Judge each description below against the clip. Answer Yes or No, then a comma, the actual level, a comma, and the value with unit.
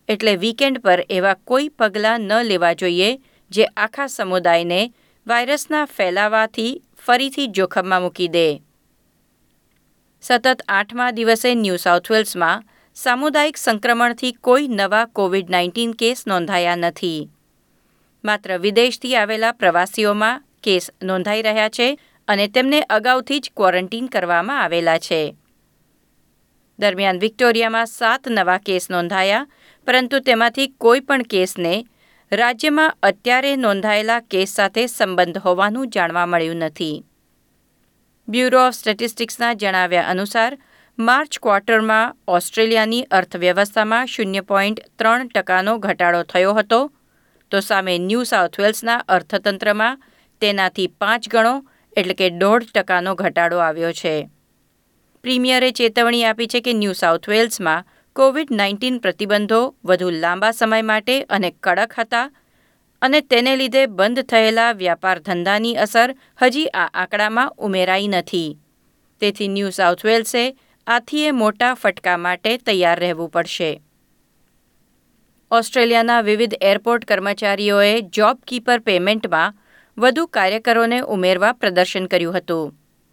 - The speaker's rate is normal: Yes, average, 110 wpm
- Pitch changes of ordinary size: Yes, average, 4.4 semitones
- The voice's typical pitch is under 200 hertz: No, high, 215 Hz